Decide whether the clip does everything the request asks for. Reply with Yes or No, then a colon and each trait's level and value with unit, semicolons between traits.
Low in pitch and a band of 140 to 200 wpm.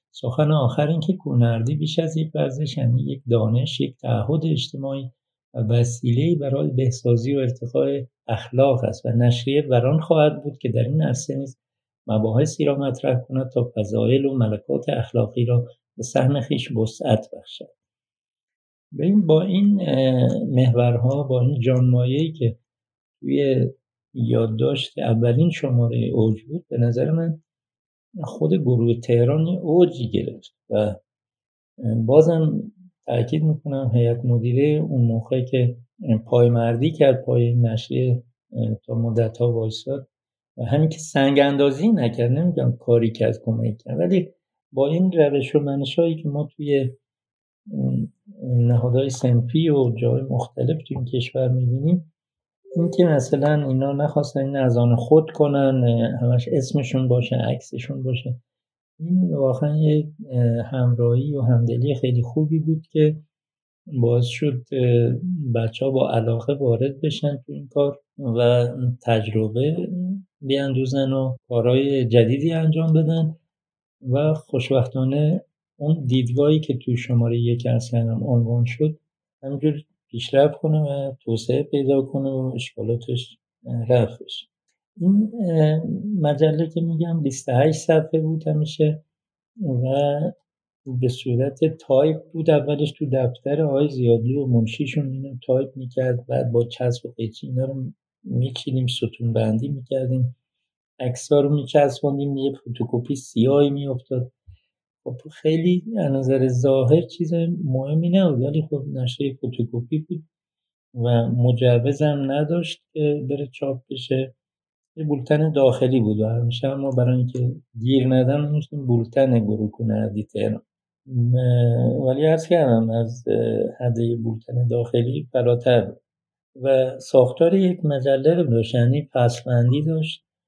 No: low, 130 Hz; average, 130 wpm